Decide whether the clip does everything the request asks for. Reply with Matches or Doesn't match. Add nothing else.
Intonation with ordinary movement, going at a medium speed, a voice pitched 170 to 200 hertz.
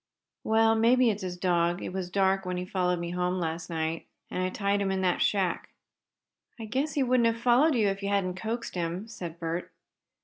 Doesn't match